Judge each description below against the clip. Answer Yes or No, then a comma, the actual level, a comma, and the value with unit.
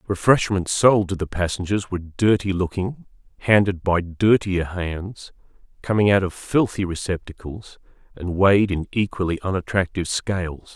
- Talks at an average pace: No, slow, 130 wpm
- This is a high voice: No, very low, 95 Hz